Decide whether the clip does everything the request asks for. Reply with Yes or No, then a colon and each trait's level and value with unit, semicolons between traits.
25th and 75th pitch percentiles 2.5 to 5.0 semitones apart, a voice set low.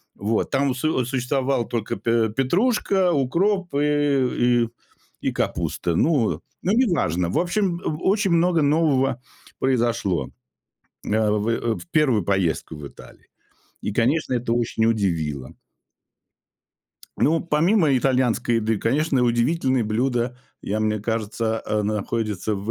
No: wide, 5.6 semitones; low, 125 Hz